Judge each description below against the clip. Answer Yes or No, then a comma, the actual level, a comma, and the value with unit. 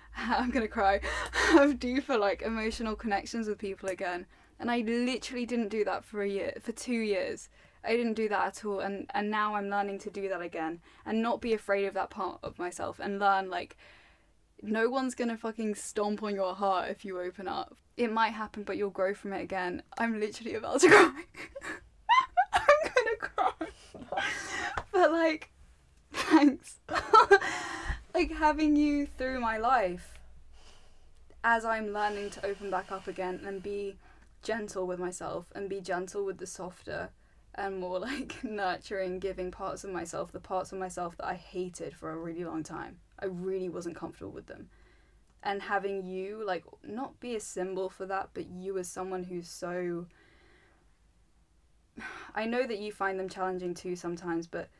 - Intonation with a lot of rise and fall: No, average, 3.9 semitones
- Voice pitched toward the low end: No, high, 200 Hz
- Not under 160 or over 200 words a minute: Yes, average, 175 wpm